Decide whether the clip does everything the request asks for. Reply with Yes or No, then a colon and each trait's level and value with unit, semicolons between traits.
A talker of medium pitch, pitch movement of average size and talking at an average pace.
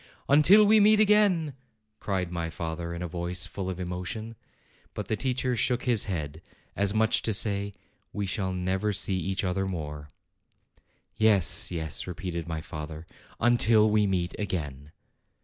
No: very low, 95 Hz; average, 4.3 semitones; average, 155 wpm